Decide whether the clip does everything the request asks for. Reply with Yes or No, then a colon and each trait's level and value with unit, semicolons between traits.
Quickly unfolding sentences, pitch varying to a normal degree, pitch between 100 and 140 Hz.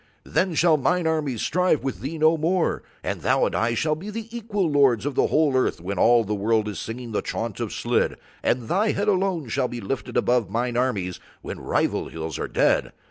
No: fast, 215 wpm; wide, 6.6 semitones; low, 135 Hz